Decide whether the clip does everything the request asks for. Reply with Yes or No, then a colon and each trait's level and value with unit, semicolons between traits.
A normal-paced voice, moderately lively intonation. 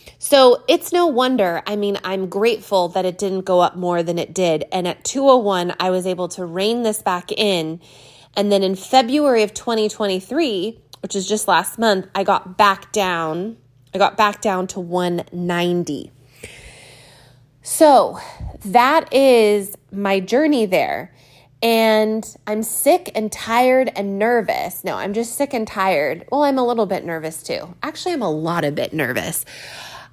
Yes: average, 165 wpm; average, 4.3 semitones